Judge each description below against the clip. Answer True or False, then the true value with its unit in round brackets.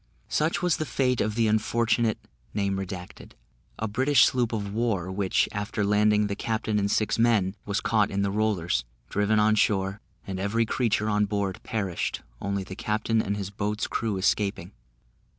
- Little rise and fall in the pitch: True (2.1 semitones)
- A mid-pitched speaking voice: False (105 Hz)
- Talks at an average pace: True (165 wpm)